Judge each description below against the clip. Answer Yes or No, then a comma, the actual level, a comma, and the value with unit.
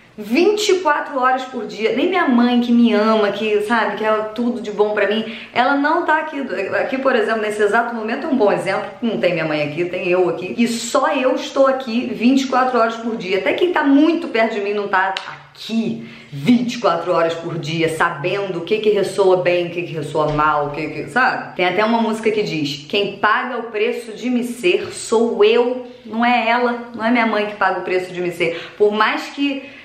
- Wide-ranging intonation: No, average, 4.3 semitones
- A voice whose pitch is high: Yes, high, 220 Hz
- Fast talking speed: Yes, fast, 225 wpm